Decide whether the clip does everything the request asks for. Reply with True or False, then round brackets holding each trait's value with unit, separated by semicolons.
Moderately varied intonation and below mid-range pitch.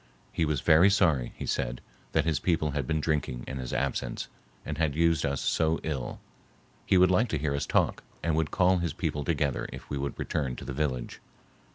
True (3.1 semitones; 75 Hz)